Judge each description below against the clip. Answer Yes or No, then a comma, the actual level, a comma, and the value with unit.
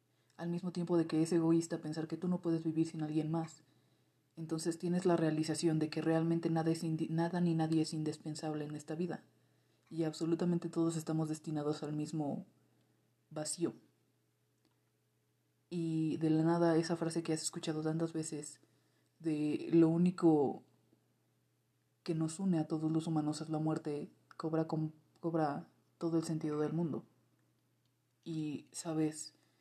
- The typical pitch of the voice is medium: Yes, medium, 160 Hz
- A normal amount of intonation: No, narrow, 1.5 semitones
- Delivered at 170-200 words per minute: No, average, 155 wpm